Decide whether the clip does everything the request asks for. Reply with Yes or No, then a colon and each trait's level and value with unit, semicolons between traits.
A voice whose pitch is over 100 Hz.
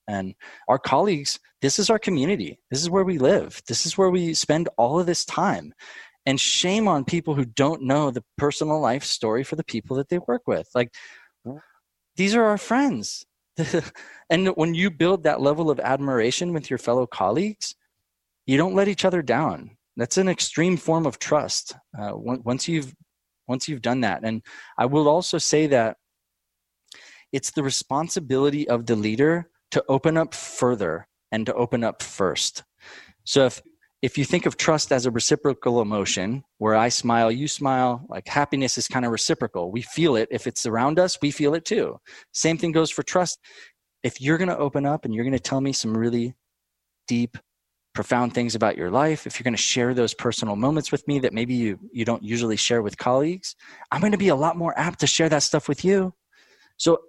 Yes: medium, 140 Hz